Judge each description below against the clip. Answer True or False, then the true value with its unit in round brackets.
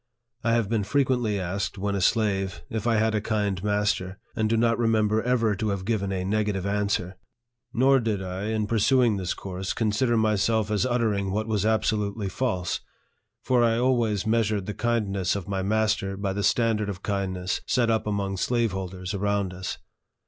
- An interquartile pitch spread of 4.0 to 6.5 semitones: False (2.6 semitones)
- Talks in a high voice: False (105 Hz)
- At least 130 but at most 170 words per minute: False (180 wpm)